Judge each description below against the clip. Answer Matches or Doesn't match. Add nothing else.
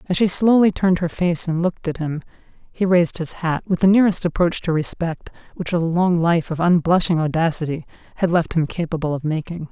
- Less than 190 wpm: Doesn't match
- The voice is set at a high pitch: Doesn't match